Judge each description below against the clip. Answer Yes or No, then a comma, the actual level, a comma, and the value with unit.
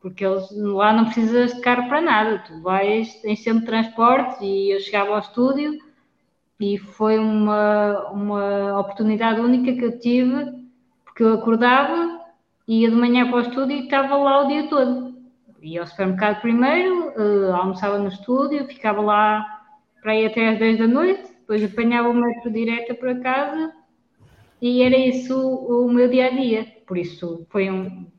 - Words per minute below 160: No, average, 165 wpm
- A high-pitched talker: Yes, high, 230 Hz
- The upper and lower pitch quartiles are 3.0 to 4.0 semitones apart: Yes, average, 3.4 semitones